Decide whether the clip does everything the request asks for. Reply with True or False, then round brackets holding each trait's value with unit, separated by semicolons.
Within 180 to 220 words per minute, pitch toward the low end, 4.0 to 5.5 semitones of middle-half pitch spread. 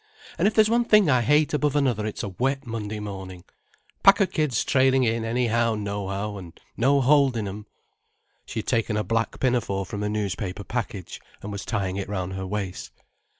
True (185 wpm; 110 Hz; 4.8 semitones)